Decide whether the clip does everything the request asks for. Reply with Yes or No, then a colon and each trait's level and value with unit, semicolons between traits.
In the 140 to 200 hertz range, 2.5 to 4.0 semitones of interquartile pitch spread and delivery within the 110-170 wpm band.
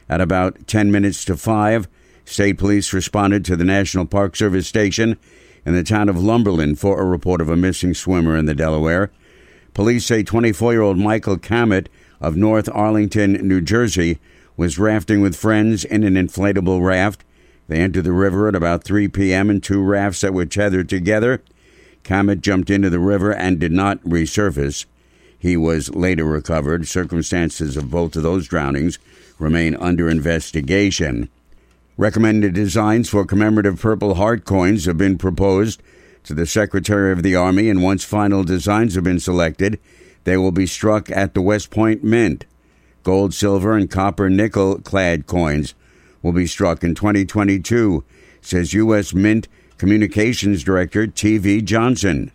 No: very low, 95 Hz; average, 3.2 semitones; average, 160 wpm